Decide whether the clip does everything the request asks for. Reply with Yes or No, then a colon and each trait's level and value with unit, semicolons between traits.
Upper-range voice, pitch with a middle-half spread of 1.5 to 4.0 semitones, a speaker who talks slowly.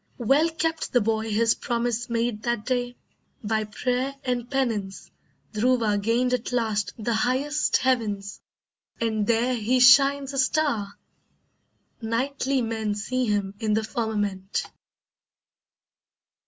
Yes: high, 235 Hz; average, 2.9 semitones; slow, 120 wpm